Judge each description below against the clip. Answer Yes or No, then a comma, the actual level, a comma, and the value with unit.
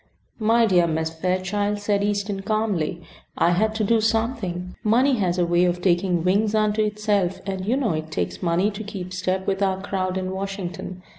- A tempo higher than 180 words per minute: Yes, average, 190 wpm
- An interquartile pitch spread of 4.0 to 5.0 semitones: No, average, 2.8 semitones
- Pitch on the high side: Yes, high, 195 Hz